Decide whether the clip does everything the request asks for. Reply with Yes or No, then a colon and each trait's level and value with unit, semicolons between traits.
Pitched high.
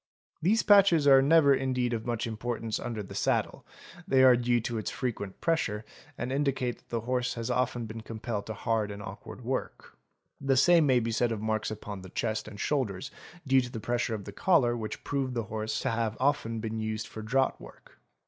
No: low, 120 Hz